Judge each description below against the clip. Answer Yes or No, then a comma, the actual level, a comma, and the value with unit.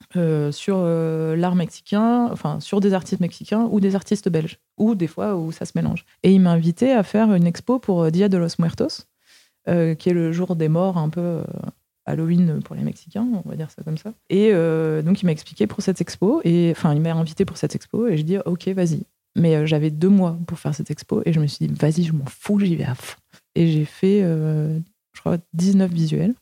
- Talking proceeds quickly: Yes, fast, 240 wpm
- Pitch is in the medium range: Yes, medium, 175 Hz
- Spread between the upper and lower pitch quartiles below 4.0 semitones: Yes, average, 3.3 semitones